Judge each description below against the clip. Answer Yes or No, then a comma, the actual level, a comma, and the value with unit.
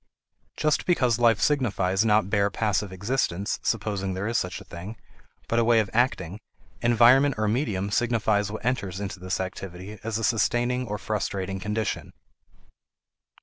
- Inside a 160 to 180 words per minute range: No, average, 150 wpm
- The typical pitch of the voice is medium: No, low, 105 Hz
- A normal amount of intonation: Yes, average, 3.4 semitones